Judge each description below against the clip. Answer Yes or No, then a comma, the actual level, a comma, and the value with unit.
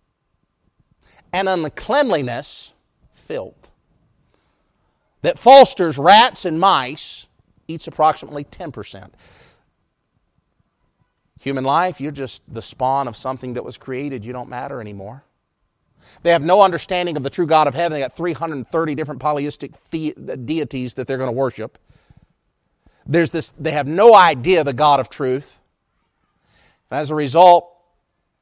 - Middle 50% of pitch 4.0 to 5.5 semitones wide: Yes, average, 4.4 semitones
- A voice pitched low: No, medium, 150 Hz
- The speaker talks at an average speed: No, slow, 130 wpm